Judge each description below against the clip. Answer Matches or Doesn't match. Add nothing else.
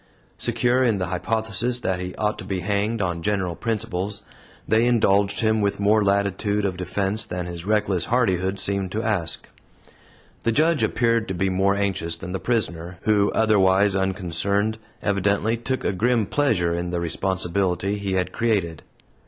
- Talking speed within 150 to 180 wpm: Matches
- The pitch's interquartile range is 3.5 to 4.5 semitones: Doesn't match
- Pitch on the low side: Matches